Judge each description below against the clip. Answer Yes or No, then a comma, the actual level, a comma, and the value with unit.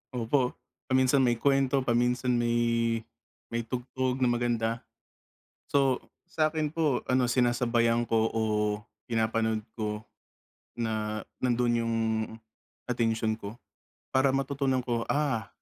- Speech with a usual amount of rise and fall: No, narrow, 2.3 semitones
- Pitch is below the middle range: Yes, low, 120 Hz